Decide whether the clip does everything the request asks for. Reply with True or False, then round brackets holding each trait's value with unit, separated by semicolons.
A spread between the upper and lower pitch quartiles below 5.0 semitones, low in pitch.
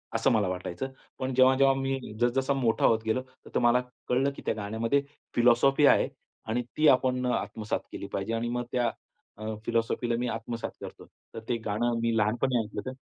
True (2.4 semitones; 120 Hz)